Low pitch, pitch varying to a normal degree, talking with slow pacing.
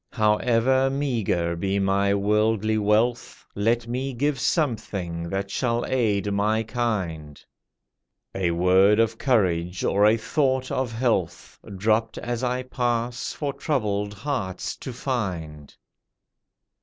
Yes: low, 110 Hz; average, 3.9 semitones; slow, 120 wpm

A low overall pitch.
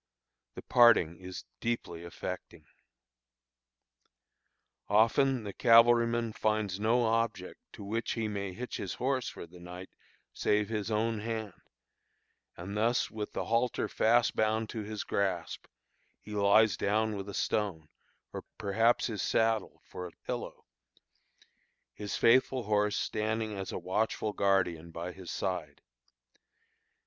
Yes: low, 105 Hz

